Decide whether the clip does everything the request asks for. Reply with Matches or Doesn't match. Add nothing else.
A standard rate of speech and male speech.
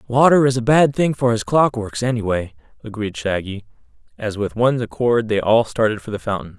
Matches